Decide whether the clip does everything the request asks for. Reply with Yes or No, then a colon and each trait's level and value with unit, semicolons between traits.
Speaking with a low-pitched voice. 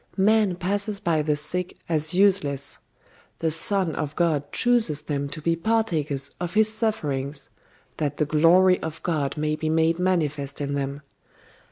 No: medium, 160 Hz